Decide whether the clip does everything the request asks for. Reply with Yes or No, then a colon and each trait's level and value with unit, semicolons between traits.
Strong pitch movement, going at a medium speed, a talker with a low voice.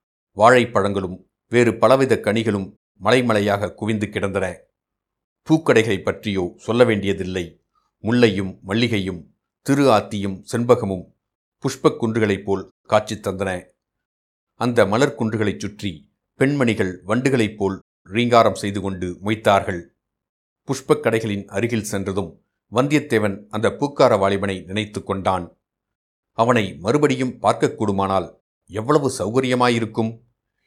No: average, 3.6 semitones; average, 90 wpm; low, 105 Hz